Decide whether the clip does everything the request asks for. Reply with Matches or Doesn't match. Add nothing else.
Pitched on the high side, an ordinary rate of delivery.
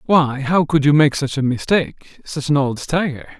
Doesn't match